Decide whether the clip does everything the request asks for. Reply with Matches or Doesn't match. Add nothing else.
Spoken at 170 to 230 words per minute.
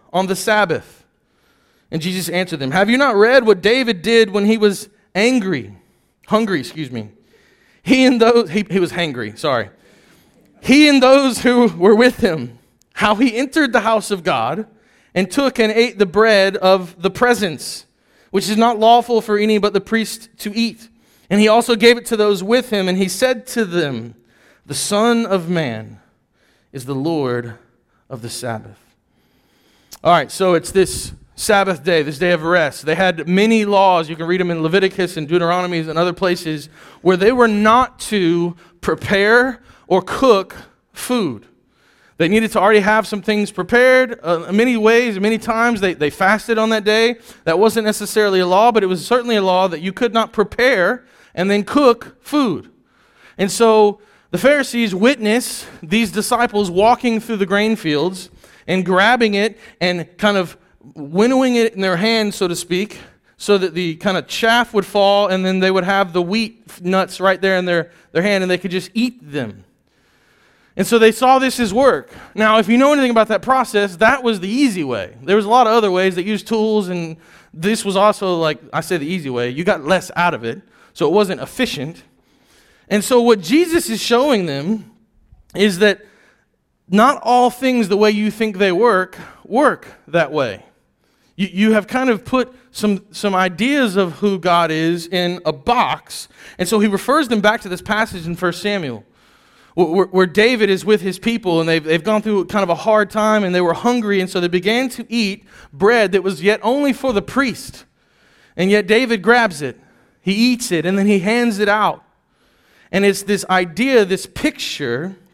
Matches